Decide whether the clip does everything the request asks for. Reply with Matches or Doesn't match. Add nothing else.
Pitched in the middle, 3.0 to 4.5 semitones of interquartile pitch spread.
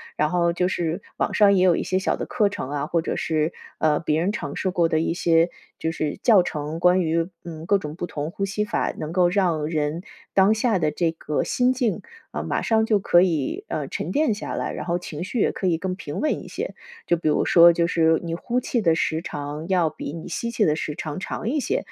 Matches